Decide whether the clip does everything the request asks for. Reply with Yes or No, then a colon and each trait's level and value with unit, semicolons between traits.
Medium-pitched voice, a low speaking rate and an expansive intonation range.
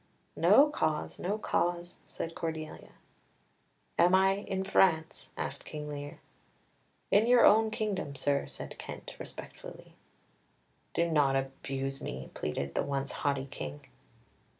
Yes: medium, 160 Hz; slow, 120 wpm; wide, 5.7 semitones